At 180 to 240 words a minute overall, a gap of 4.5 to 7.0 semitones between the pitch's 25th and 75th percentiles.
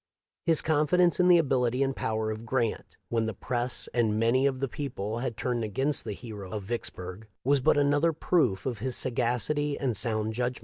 No: average, 195 wpm; average, 4.1 semitones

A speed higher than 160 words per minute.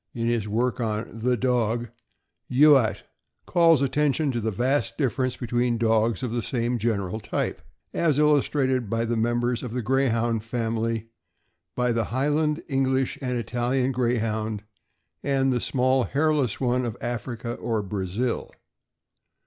No: average, 140 wpm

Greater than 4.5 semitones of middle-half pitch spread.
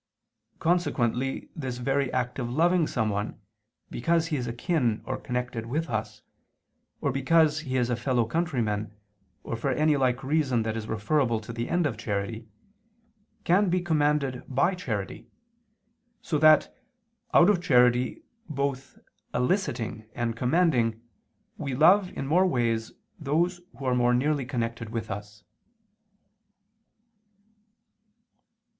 Yes: average, 5.1 semitones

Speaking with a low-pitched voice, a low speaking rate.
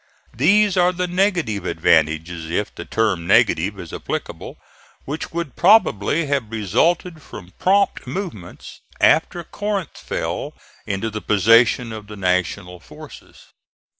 Yes: low, 115 Hz; slow, 125 wpm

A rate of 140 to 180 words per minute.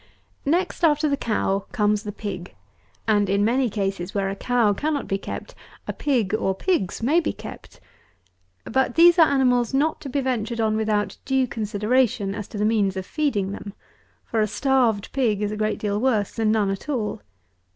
No: average, 195 wpm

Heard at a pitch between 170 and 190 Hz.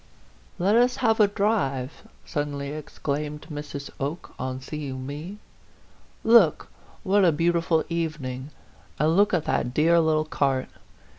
No: medium, 155 Hz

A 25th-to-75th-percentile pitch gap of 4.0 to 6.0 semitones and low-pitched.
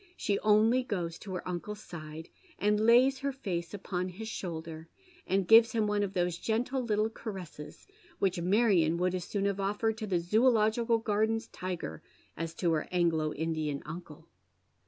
No: average, 4.4 semitones; high, 195 Hz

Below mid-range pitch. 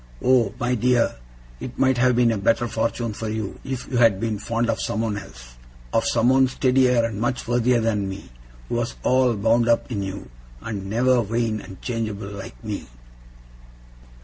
Yes: low, 115 Hz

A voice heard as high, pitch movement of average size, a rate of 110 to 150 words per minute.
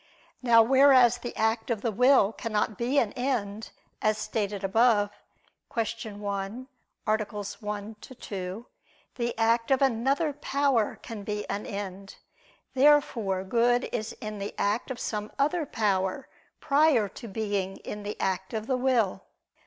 Yes: high, 225 Hz; average, 3.5 semitones; average, 145 wpm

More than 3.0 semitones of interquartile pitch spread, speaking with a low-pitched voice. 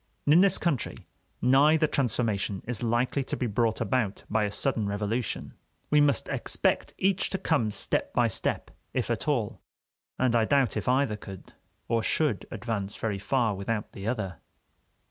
Yes: average, 4.6 semitones; low, 115 Hz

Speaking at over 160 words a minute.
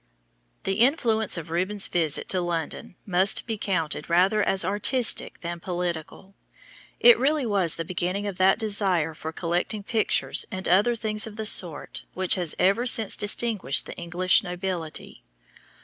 No: average, 150 wpm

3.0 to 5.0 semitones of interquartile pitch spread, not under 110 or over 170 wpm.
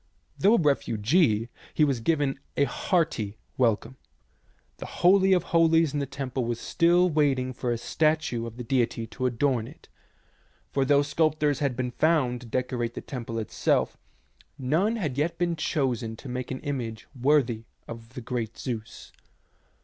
Yes: average, 4.5 semitones; average, 160 wpm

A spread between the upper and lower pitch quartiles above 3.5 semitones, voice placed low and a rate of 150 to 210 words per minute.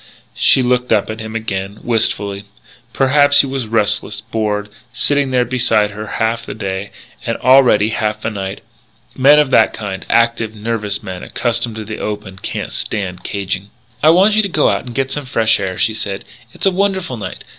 Yes: average, 3.9 semitones; low, 110 Hz; average, 190 wpm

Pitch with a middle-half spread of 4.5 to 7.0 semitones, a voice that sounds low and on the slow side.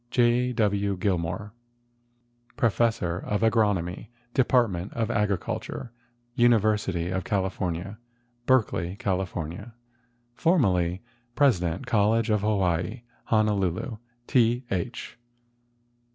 No: average, 4.1 semitones; low, 105 Hz; slow, 80 wpm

